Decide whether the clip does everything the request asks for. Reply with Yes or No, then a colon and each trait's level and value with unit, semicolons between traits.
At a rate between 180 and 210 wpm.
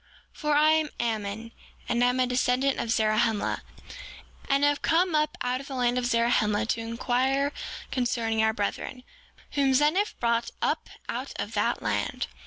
No: average, 160 wpm